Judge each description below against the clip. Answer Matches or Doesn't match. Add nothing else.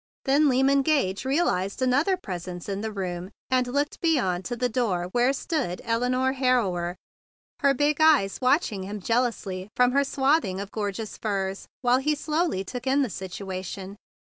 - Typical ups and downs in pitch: Doesn't match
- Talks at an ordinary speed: Matches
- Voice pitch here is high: Matches